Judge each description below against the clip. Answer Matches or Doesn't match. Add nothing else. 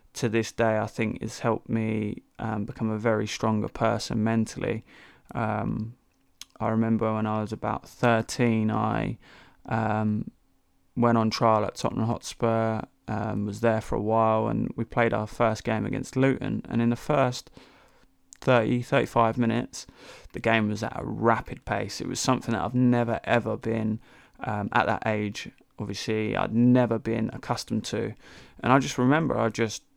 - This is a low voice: Matches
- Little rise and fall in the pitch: Matches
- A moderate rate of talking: Matches